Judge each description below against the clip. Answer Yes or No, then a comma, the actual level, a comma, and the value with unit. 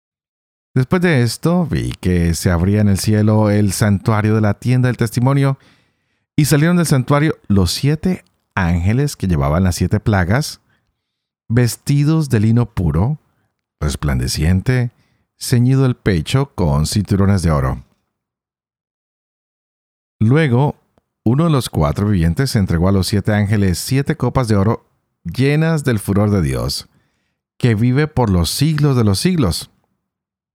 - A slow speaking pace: No, average, 135 wpm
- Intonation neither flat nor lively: No, wide, 6.1 semitones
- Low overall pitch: Yes, low, 115 Hz